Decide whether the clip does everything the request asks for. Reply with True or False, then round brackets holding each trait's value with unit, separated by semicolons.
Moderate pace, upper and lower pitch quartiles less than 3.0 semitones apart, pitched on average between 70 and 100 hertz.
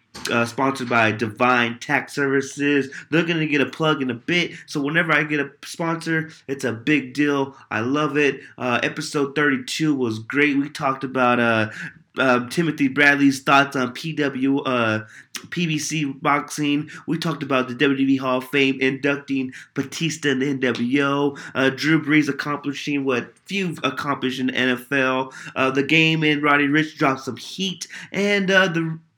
False (170 wpm; 2.6 semitones; 140 Hz)